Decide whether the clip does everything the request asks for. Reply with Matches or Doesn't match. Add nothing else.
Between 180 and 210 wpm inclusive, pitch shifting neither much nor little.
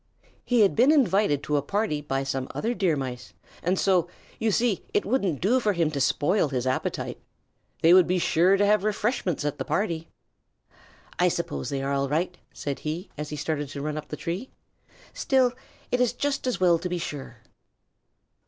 Doesn't match